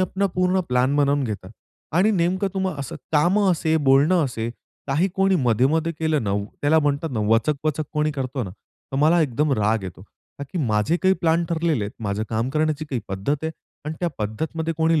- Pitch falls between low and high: Yes, medium, 150 Hz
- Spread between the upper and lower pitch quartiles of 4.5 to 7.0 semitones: Yes, average, 4.9 semitones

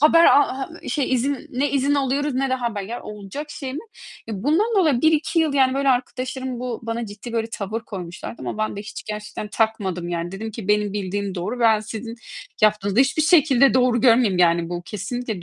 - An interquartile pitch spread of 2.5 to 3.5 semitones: No, average, 4.6 semitones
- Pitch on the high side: Yes, high, 235 Hz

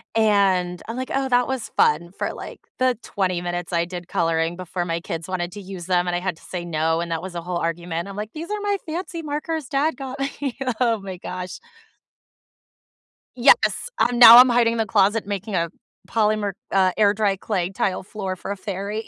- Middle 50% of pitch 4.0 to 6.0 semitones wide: Yes, average, 5.1 semitones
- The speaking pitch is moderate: No, high, 195 Hz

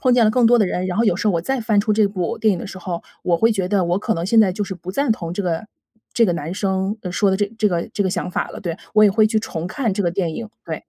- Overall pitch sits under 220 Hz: Yes, high, 200 Hz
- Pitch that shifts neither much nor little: Yes, average, 3.4 semitones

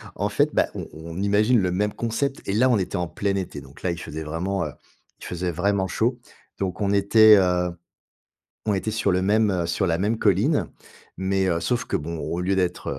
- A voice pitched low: Yes, very low, 95 Hz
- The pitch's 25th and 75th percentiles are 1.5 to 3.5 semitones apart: Yes, average, 2.9 semitones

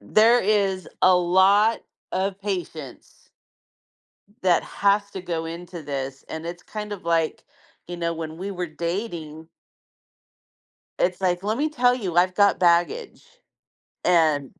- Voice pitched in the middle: Yes, medium, 180 Hz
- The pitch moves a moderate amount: Yes, average, 3.3 semitones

